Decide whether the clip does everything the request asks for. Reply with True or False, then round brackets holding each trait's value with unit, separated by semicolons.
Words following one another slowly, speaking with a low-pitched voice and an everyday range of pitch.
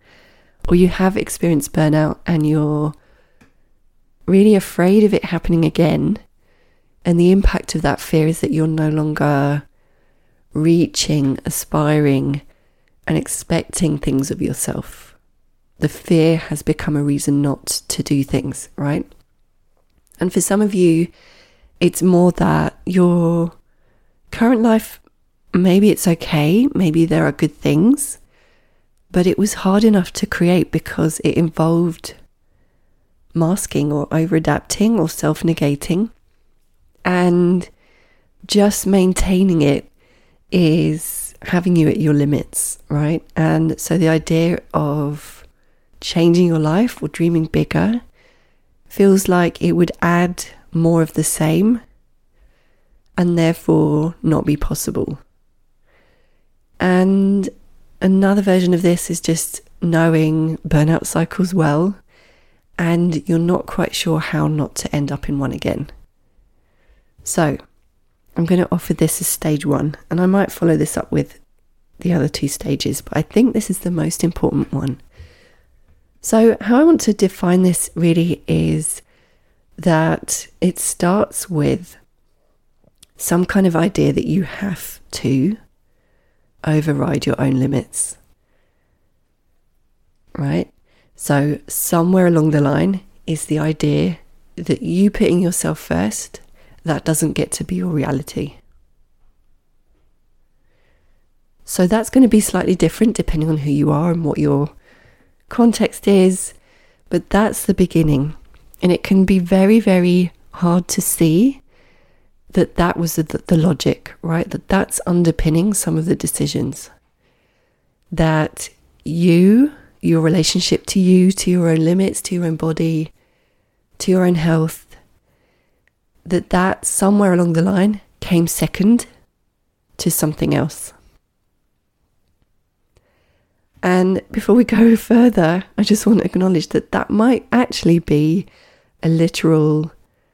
False (130 wpm; 170 Hz; 3.3 semitones)